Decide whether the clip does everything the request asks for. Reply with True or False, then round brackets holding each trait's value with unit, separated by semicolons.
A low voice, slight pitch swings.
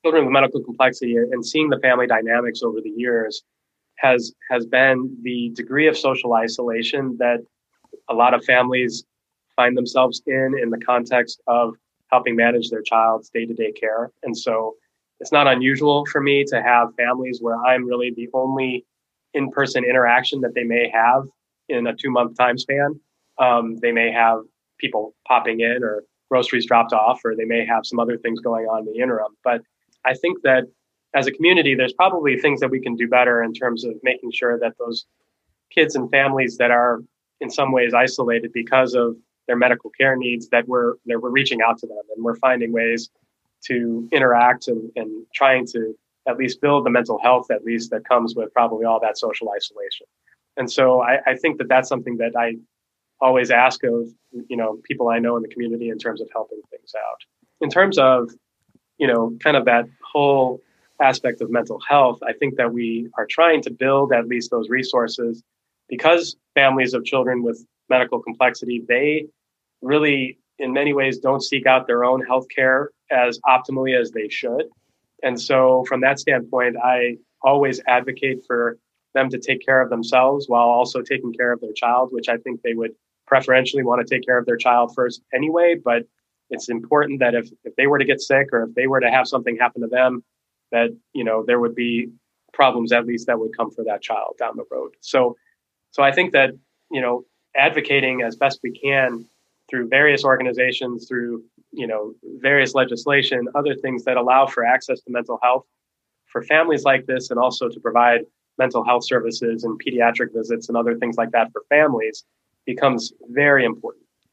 True (125 Hz; 2.1 semitones)